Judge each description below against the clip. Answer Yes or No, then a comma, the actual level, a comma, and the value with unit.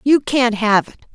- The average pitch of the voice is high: Yes, high, 235 Hz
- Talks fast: Yes, fast, 210 wpm